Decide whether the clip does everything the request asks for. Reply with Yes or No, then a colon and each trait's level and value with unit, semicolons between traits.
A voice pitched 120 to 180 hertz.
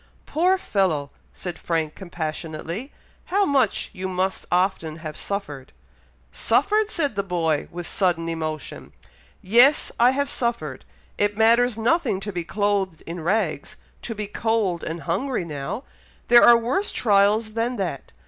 No: high, 200 Hz